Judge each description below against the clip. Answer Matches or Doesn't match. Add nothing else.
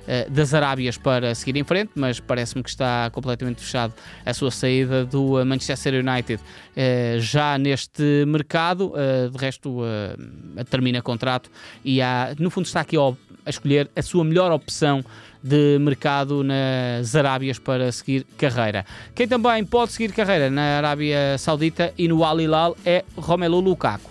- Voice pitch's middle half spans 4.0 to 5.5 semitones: Doesn't match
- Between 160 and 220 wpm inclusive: Doesn't match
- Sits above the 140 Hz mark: Doesn't match